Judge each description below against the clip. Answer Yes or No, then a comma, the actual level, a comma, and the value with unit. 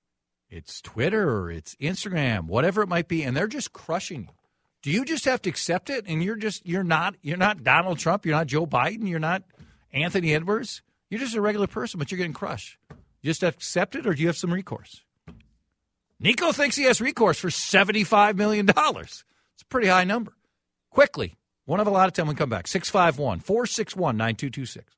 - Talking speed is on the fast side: No, average, 195 wpm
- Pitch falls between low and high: Yes, medium, 180 Hz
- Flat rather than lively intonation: No, average, 5.1 semitones